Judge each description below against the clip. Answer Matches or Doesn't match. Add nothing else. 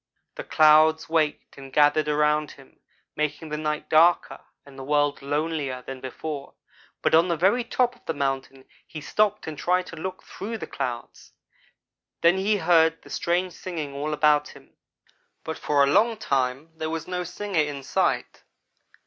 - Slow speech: Doesn't match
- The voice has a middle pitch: Matches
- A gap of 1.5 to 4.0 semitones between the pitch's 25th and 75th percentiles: Matches